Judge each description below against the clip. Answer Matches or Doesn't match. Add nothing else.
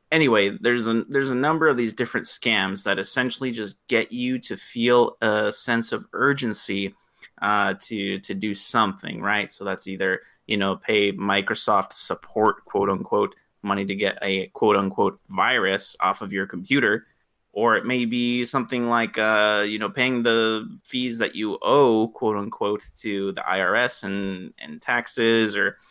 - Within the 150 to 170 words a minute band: Matches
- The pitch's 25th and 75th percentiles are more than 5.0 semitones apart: Doesn't match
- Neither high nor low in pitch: Doesn't match